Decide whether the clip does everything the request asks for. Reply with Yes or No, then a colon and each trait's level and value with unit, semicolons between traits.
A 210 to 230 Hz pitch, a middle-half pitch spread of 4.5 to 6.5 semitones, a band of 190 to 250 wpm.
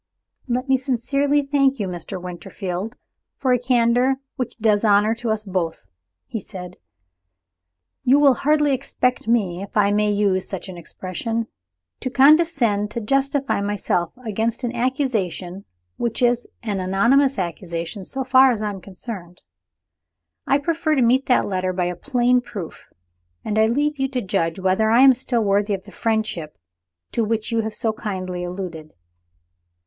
No: high, 220 Hz; average, 5.1 semitones; average, 160 wpm